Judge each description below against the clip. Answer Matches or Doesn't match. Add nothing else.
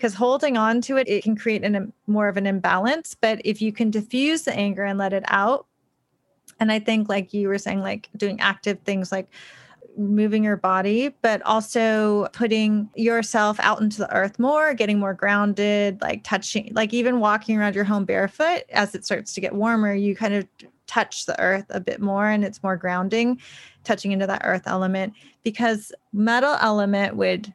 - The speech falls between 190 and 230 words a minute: Matches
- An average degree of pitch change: Doesn't match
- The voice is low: Doesn't match